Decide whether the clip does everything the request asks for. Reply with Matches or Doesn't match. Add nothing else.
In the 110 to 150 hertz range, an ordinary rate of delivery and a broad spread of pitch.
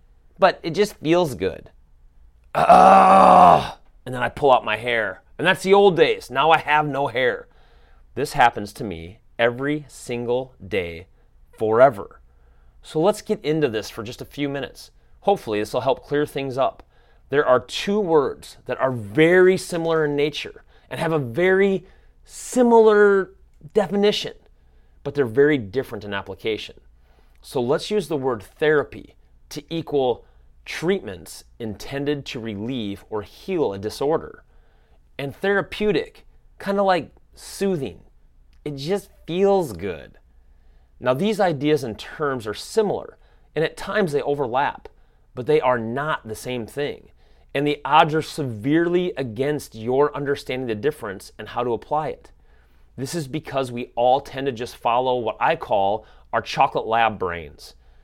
Matches